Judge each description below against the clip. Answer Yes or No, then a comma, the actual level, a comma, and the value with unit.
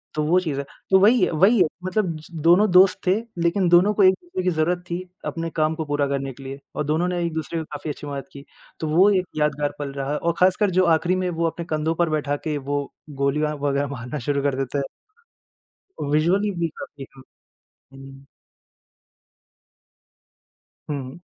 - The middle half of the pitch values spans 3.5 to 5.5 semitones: Yes, average, 4.0 semitones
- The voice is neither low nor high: Yes, medium, 155 Hz